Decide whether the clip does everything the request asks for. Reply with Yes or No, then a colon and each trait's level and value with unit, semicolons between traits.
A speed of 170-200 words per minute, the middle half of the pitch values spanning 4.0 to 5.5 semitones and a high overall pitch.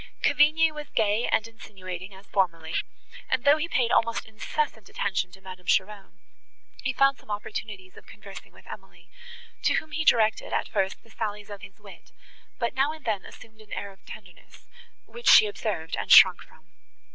Yes: average, 180 wpm; average, 4.3 semitones; high, 215 Hz